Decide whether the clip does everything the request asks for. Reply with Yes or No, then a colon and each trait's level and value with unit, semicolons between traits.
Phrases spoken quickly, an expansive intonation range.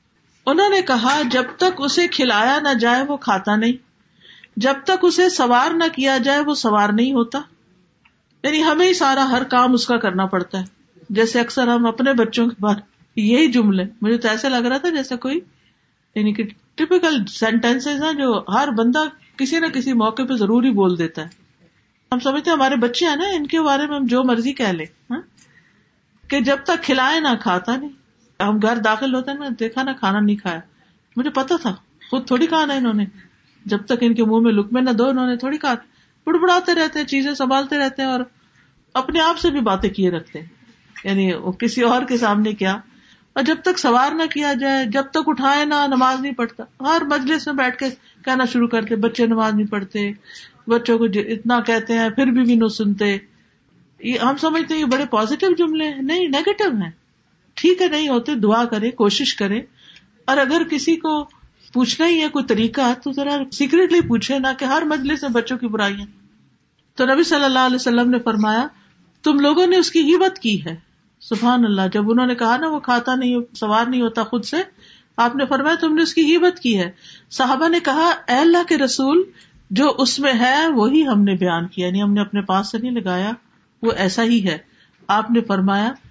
No: fast, 205 wpm; average, 4.4 semitones